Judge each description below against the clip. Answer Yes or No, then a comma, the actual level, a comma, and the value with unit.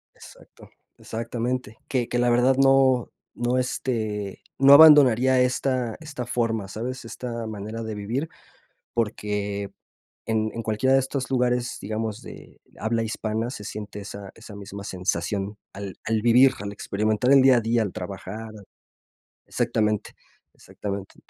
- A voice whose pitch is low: Yes, low, 115 Hz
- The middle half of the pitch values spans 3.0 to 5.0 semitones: Yes, average, 3.3 semitones